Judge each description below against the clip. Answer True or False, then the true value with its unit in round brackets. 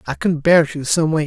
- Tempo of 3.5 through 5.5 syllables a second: False (5.8 syllables/s)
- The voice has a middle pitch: True (150 Hz)